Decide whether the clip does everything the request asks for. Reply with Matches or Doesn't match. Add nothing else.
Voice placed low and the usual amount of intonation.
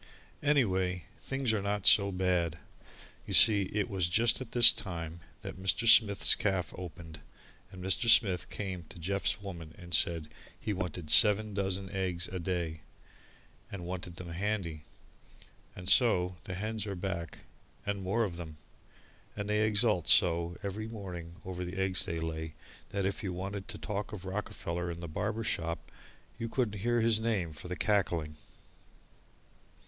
Matches